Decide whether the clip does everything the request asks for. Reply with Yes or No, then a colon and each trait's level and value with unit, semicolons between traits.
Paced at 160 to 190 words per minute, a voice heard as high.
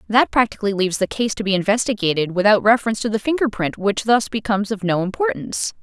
No: fast, 205 wpm; high, 210 Hz